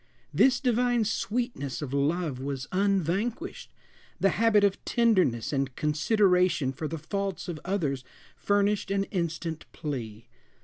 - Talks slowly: Yes, slow, 125 wpm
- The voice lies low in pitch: No, medium, 180 Hz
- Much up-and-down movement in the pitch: Yes, wide, 5.8 semitones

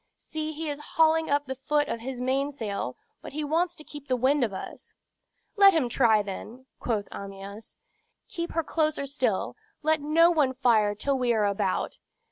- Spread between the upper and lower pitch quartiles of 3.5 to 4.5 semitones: No, average, 5.3 semitones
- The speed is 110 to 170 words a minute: No, average, 180 wpm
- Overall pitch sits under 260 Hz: No, very high, 275 Hz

